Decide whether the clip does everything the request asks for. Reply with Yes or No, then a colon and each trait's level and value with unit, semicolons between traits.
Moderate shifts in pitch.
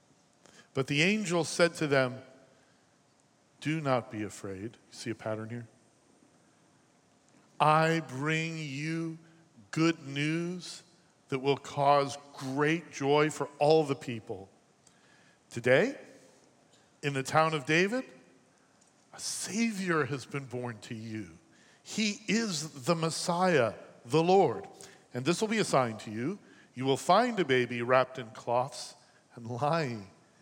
Yes: average, 4.7 semitones